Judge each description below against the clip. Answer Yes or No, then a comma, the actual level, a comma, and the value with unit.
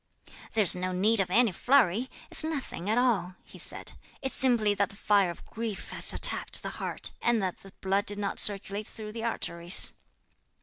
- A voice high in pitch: Yes, high, 205 Hz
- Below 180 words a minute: No, average, 185 wpm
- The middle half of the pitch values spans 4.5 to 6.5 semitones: No, average, 3.4 semitones